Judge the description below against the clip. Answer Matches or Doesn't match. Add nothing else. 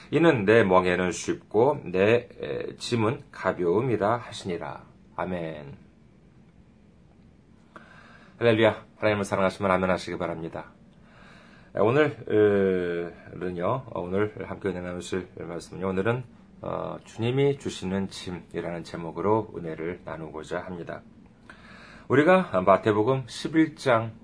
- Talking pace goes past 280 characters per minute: Doesn't match